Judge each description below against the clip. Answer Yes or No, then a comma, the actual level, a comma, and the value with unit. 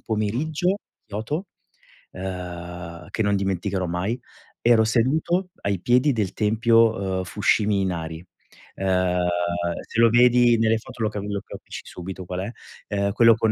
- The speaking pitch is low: Yes, low, 105 Hz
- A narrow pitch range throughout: No, average, 3.8 semitones